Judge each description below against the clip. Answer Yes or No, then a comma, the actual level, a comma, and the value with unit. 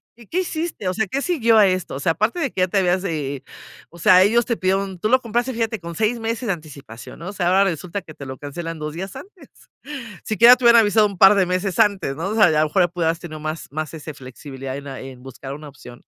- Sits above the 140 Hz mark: Yes, medium, 185 Hz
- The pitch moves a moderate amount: No, wide, 5.9 semitones